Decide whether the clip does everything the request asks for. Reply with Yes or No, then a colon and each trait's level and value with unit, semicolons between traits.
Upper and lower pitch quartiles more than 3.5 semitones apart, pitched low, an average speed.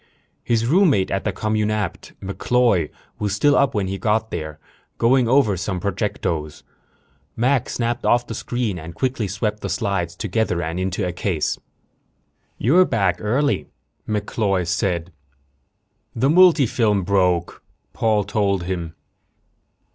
No: average, 4.4 semitones; low, 105 Hz; slow, 130 wpm